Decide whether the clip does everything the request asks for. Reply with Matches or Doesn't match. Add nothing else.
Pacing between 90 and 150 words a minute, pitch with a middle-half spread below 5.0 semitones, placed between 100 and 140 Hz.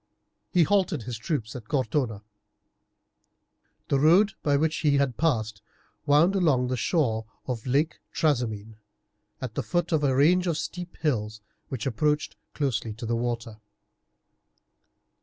Doesn't match